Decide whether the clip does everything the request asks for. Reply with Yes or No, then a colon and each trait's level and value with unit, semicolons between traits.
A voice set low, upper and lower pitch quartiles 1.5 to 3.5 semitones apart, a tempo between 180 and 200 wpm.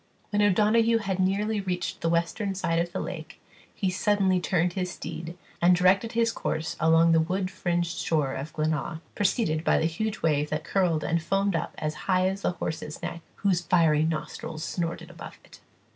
No: medium, 175 Hz; average, 3.1 semitones; average, 185 wpm